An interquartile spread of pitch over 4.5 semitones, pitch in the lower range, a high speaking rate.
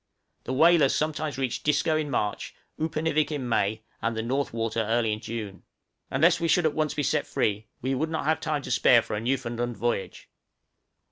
No: average, 5.3 semitones; low, 130 Hz; average, 195 wpm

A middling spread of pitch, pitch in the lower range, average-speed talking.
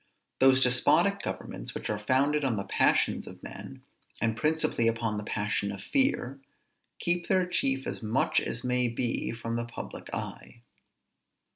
Yes: average, 3.0 semitones; low, 120 Hz; average, 155 wpm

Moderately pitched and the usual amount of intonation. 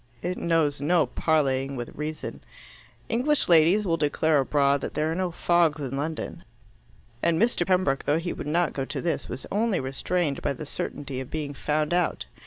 Yes: medium, 155 Hz; average, 3.5 semitones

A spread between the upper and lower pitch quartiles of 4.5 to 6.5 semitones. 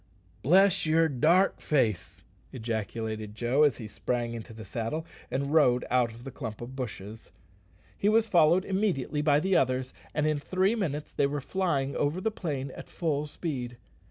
Yes: wide, 5.4 semitones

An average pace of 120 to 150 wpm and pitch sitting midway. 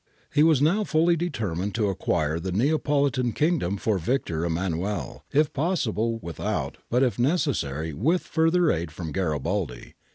No: average, 140 wpm; low, 115 Hz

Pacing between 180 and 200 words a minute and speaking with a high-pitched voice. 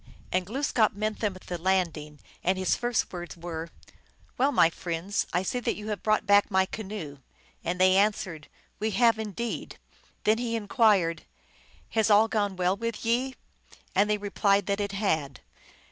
Yes: average, 185 wpm; high, 200 Hz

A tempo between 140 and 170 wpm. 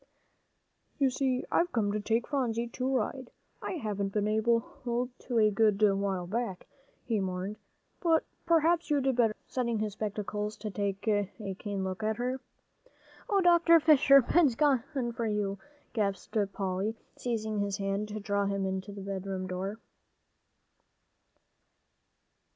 Yes: average, 145 wpm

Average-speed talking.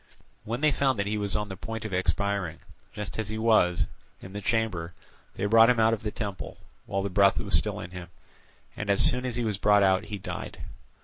No: fast, 230 wpm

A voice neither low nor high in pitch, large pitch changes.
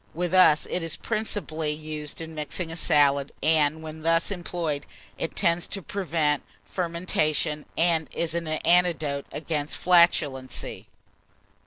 No: medium, 160 Hz; narrow, 2.4 semitones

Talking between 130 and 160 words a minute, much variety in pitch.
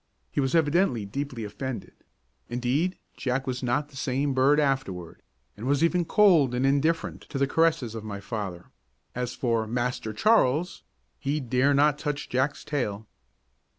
No: average, 150 wpm; average, 3.5 semitones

